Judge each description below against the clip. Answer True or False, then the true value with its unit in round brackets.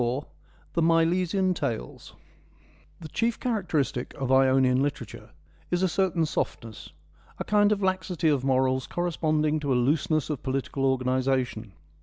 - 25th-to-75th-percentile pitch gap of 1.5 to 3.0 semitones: False (5.1 semitones)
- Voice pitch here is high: False (150 Hz)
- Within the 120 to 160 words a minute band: True (140 wpm)